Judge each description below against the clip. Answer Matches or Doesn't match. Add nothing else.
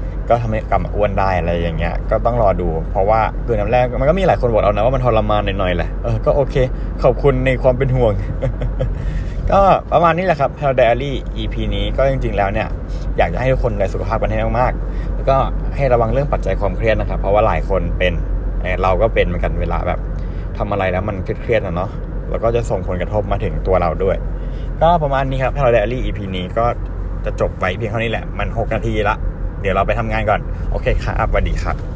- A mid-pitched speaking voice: Doesn't match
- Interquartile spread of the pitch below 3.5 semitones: Doesn't match